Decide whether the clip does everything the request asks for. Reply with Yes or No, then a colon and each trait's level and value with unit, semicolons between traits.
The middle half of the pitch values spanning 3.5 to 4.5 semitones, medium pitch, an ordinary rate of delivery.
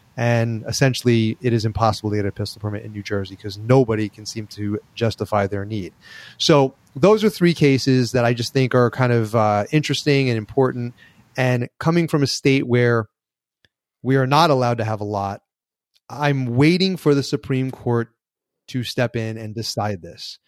No: average, 3.8 semitones; low, 120 Hz; average, 185 wpm